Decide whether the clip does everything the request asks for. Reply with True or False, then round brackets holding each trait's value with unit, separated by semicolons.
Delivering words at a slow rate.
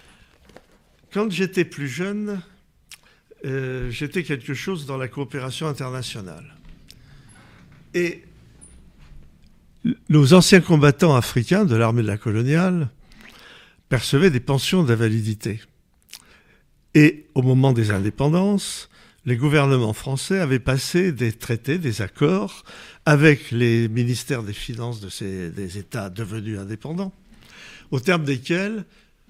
True (110 wpm)